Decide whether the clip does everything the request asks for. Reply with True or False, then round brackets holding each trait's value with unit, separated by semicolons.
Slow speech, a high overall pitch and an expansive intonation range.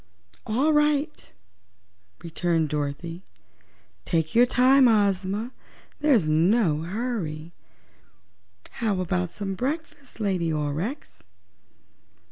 True (85 wpm; 195 Hz; 7.2 semitones)